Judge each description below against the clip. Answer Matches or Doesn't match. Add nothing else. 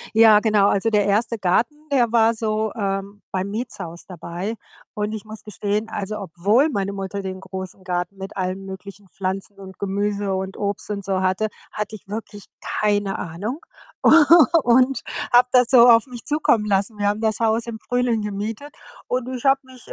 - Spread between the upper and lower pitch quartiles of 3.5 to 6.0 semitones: Doesn't match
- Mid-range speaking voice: Doesn't match